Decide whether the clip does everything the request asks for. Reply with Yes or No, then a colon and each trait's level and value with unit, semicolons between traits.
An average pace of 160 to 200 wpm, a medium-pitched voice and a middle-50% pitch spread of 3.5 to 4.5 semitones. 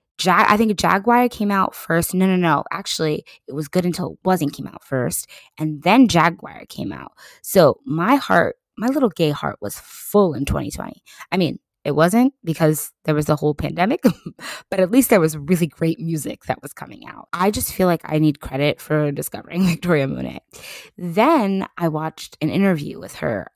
Yes: average, 195 wpm; medium, 170 Hz; average, 4.0 semitones